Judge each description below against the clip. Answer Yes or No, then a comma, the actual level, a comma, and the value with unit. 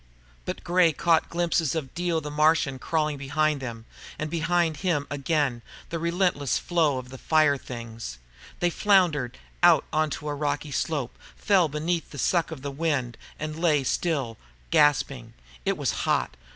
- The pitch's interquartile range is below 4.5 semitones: Yes, average, 3.4 semitones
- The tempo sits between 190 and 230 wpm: No, average, 160 wpm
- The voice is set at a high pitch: No, medium, 150 Hz